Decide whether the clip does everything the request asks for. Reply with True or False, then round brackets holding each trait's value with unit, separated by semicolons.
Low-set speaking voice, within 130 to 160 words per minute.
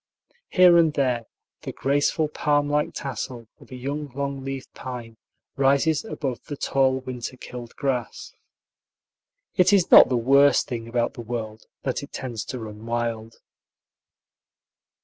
True (130 Hz; 145 wpm)